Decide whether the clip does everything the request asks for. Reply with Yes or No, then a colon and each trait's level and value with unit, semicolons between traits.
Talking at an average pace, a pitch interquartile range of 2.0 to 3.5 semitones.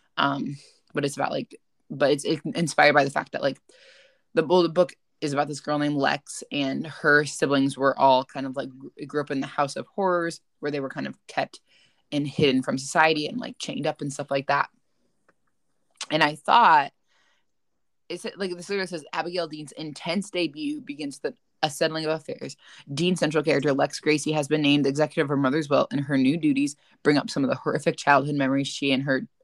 No: fast, 210 wpm; average, 3.0 semitones